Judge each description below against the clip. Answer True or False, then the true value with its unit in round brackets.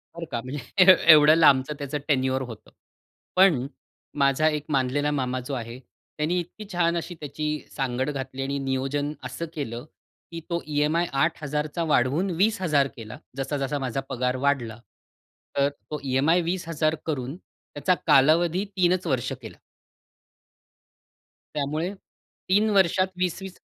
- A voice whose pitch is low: False (150 Hz)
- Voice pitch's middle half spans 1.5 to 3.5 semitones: False (4.1 semitones)